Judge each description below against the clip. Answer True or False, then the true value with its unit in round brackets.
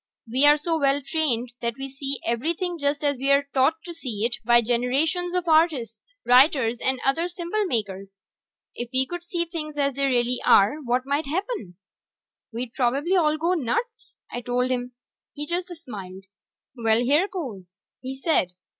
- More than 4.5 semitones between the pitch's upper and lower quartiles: True (5.1 semitones)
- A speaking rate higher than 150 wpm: True (170 wpm)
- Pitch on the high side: True (275 Hz)